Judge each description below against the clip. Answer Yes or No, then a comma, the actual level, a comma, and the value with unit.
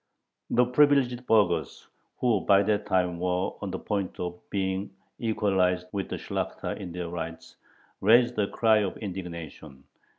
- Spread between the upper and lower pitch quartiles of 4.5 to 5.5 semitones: No, average, 3.4 semitones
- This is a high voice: No, very low, 95 Hz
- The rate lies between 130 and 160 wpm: Yes, average, 145 wpm